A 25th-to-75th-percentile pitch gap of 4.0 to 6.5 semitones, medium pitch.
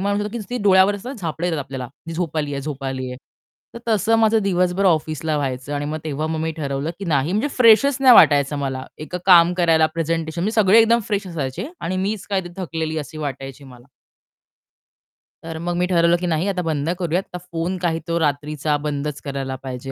Yes: average, 4.5 semitones; medium, 165 Hz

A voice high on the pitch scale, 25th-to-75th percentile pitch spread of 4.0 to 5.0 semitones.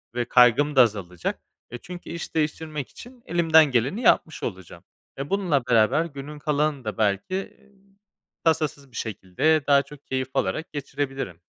No: medium, 140 Hz; average, 4.7 semitones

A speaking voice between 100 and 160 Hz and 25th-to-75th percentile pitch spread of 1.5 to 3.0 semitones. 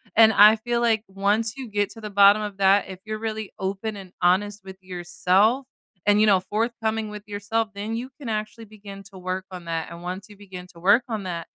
No: high, 205 Hz; narrow, 2.5 semitones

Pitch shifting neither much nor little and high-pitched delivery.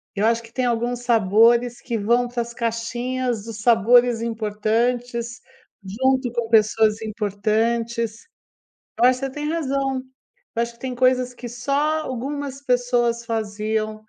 No: narrow, 2.0 semitones; high, 235 Hz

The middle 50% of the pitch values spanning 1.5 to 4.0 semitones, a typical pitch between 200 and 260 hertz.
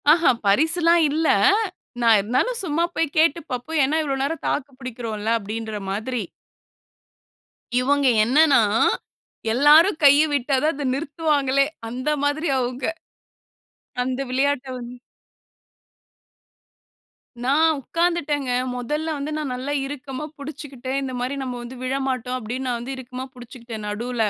No: average, 3.3 semitones; very high, 270 Hz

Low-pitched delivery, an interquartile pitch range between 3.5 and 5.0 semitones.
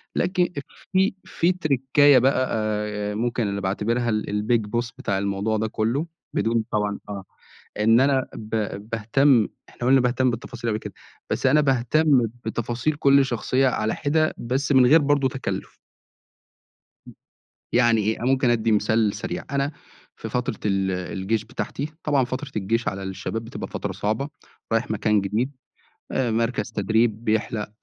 Yes: low, 115 Hz; average, 3.9 semitones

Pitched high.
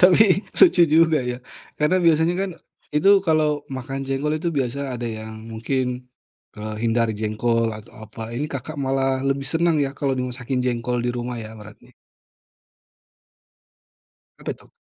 No: low, 130 Hz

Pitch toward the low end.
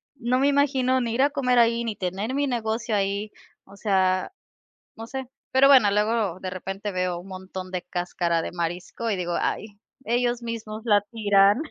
No: high, 215 Hz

